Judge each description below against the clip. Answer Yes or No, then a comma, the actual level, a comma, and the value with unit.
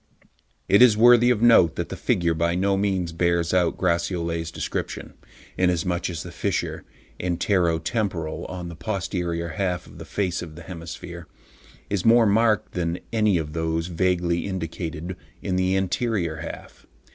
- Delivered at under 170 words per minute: Yes, average, 155 wpm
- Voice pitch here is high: No, very low, 90 Hz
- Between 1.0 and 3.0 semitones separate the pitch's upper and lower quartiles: Yes, average, 2.7 semitones